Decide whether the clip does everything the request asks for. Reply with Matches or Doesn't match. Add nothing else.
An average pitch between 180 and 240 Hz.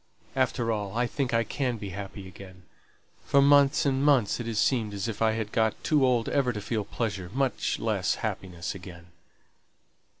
Doesn't match